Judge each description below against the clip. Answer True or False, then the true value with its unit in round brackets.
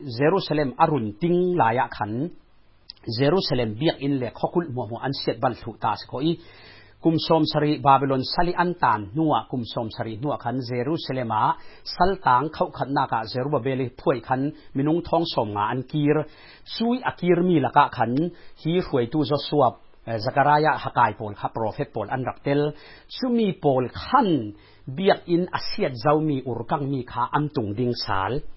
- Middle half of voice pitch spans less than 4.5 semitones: False (4.9 semitones)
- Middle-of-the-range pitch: True (145 Hz)